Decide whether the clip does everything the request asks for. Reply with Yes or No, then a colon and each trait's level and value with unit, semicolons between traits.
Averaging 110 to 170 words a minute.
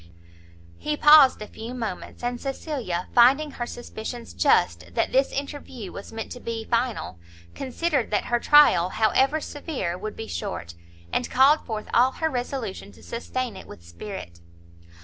Yes: average, 155 wpm